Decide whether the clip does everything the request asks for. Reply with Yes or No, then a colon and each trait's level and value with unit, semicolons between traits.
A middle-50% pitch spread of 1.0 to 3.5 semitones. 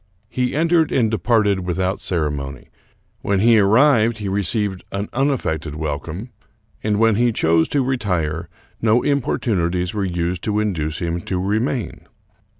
No: average, 5.2 semitones